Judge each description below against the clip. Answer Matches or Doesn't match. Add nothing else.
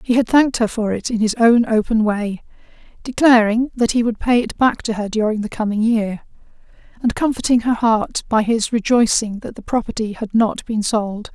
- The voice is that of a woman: Matches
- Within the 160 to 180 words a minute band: Doesn't match